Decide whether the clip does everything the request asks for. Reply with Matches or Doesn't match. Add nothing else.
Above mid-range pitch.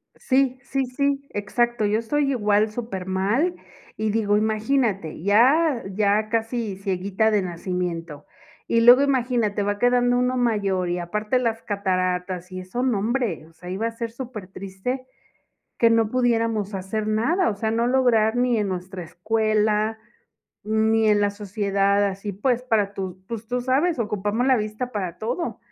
Matches